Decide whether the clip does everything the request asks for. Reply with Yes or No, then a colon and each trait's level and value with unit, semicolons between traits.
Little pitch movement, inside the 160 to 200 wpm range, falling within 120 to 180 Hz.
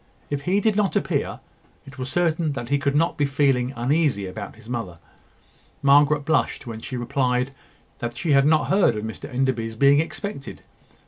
No: average, 4.0 semitones; average, 180 wpm; medium, 140 Hz